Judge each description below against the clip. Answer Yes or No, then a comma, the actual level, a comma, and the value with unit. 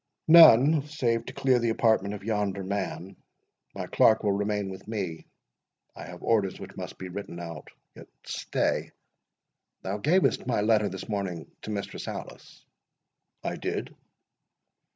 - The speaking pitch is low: Yes, low, 105 Hz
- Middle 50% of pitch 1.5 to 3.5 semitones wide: Yes, average, 3.1 semitones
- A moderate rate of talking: No, slow, 130 wpm